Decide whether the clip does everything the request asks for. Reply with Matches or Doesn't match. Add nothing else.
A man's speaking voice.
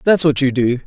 Matches